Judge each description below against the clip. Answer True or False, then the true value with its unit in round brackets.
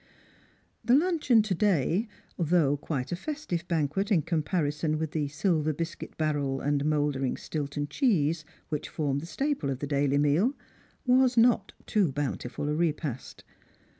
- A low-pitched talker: False (155 Hz)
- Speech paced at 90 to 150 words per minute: True (145 wpm)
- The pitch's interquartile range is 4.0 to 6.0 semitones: True (5.1 semitones)